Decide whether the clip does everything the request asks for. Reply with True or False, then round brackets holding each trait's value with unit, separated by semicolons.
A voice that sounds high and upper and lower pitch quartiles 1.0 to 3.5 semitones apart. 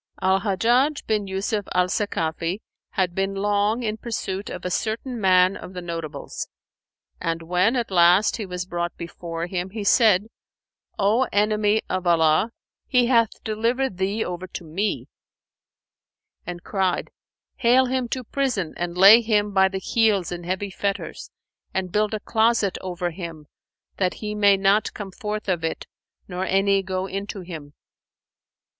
True (195 Hz; 3.1 semitones)